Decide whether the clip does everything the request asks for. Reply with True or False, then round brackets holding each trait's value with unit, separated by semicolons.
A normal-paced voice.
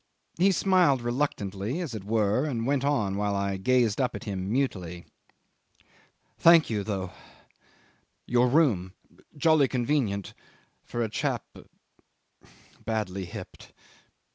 False (115 wpm)